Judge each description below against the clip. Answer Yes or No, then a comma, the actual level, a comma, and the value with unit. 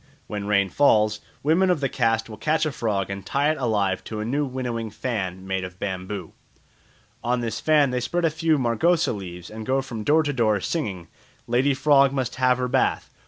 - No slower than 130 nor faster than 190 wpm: No, fast, 205 wpm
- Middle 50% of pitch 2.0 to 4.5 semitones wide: No, average, 5.3 semitones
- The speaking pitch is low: Yes, low, 120 Hz